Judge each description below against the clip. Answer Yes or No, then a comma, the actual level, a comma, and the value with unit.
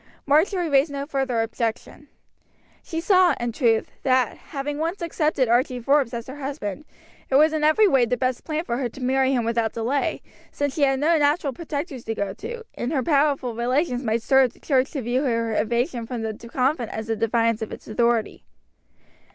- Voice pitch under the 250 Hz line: No, very high, 260 Hz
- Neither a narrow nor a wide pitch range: Yes, average, 3.9 semitones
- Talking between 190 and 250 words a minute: Yes, average, 200 wpm